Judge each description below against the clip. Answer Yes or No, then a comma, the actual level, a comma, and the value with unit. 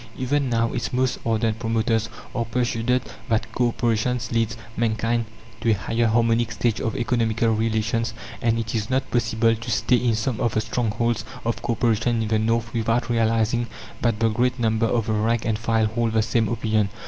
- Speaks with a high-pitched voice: No, low, 115 Hz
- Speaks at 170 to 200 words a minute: Yes, average, 190 wpm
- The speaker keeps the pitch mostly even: Yes, narrow, 1.1 semitones